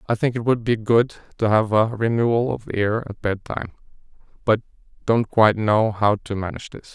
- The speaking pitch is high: No, low, 110 Hz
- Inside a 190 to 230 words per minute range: Yes, average, 200 wpm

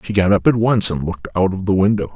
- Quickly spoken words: Yes, fast, 305 wpm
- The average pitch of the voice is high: No, low, 100 Hz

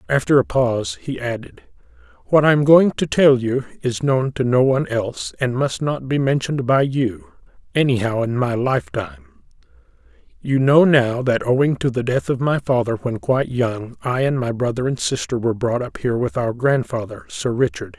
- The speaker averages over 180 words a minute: Yes, average, 190 wpm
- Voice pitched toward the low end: Yes, low, 130 Hz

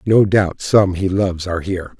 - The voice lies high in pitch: No, very low, 95 Hz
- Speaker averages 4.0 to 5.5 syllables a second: Yes, 5.4 syllables/s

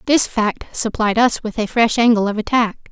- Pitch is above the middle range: Yes, high, 225 Hz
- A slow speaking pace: No, fast, 205 wpm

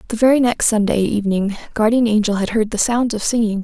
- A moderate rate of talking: No, fast, 215 wpm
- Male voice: No, female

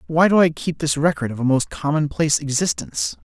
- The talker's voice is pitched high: No, medium, 155 Hz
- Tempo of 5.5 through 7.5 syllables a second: Yes, 5.9 syllables/s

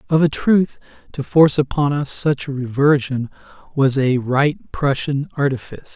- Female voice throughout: No, male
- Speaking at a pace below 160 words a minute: Yes, average, 150 wpm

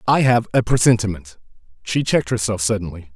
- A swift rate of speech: No, slow, 135 wpm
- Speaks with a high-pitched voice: No, low, 105 Hz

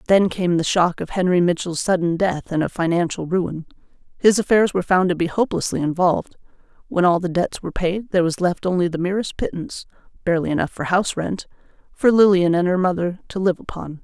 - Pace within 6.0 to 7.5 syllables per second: Yes, 6.1 syllables/s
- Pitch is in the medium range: Yes, medium, 180 Hz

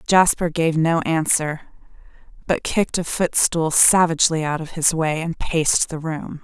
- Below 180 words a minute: Yes, average, 160 wpm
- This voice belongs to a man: No, female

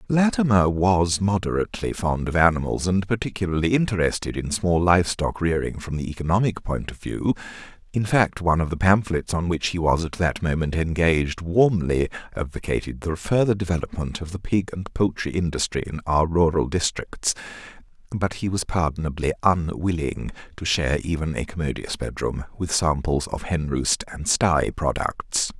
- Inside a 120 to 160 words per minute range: Yes, average, 155 wpm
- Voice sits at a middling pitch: No, very low, 85 Hz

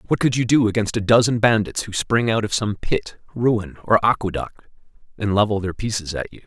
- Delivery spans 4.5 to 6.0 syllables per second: Yes, 5.4 syllables/s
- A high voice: No, low, 105 Hz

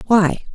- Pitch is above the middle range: Yes, high, 200 Hz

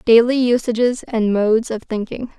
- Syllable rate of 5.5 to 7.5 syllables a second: No, 4.9 syllables/s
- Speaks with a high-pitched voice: Yes, high, 230 Hz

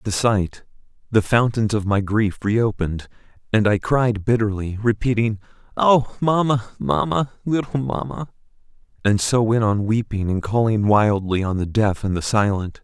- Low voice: Yes, low, 110 Hz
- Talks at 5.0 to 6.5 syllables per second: No, 4.6 syllables/s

